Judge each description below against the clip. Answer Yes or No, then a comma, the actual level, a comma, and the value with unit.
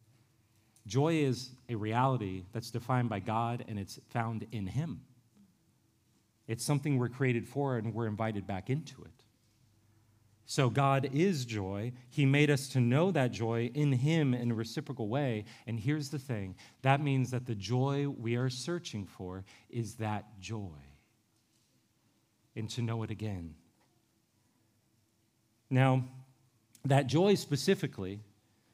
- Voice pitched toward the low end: Yes, low, 120 Hz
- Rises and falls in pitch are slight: No, average, 3.7 semitones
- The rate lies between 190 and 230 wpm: No, average, 140 wpm